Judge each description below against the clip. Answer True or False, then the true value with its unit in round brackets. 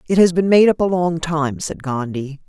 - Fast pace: True (240 wpm)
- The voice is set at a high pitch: False (165 Hz)